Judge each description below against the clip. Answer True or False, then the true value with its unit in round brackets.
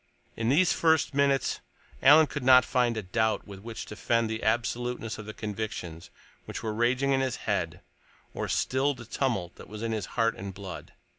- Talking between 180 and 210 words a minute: True (195 wpm)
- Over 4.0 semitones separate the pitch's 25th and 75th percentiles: False (3.6 semitones)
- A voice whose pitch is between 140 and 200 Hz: False (115 Hz)